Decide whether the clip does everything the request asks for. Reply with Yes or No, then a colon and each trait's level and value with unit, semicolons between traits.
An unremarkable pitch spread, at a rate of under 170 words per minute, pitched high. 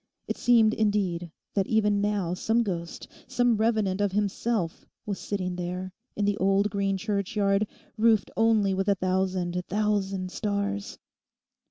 No: narrow, 2.1 semitones; average, 140 wpm; high, 200 Hz